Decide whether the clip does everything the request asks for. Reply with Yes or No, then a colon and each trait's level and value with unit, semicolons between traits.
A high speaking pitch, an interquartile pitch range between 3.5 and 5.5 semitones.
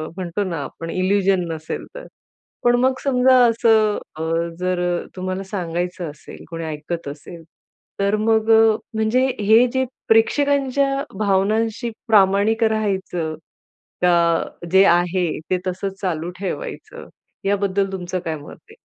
Yes: high, 195 Hz; average, 4.1 semitones